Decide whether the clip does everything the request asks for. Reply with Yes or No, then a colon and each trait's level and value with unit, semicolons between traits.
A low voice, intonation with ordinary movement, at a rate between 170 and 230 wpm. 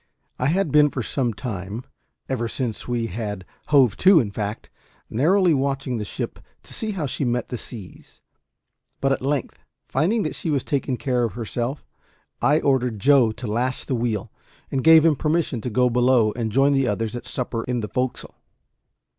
Yes: low, 125 Hz; average, 3.6 semitones; average, 185 wpm